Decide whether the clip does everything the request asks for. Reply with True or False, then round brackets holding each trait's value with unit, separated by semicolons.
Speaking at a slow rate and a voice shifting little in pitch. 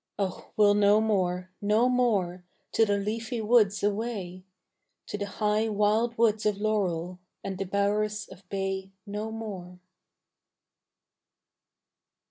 True (120 wpm; 2.1 semitones)